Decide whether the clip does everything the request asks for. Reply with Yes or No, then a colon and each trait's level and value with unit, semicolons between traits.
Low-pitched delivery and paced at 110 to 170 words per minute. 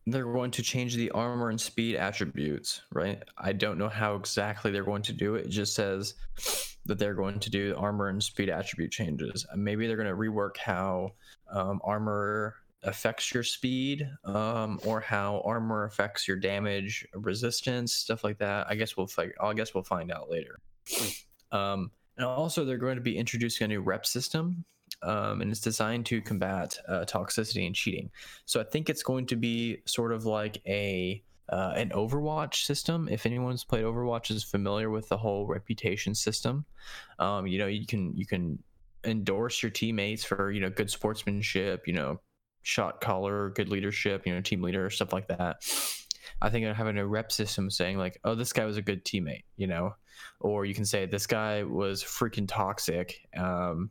No: low, 105 Hz; average, 190 wpm